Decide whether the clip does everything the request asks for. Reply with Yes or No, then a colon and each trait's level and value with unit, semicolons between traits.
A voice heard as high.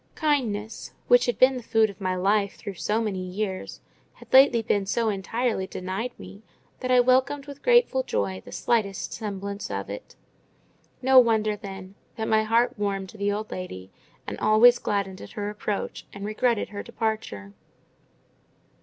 Yes: high, 215 Hz